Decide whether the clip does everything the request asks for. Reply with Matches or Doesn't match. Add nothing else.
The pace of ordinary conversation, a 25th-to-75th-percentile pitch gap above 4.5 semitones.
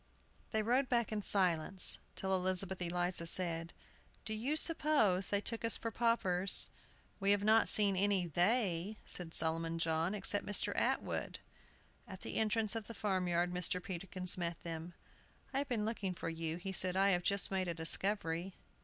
Doesn't match